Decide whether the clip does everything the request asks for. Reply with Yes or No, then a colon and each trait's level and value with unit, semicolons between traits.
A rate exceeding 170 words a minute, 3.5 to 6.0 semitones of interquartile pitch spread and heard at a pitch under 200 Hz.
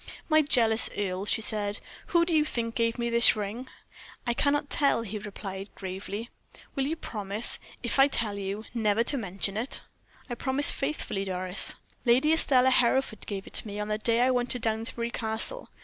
No: average, 185 wpm; average, 4.0 semitones; high, 230 Hz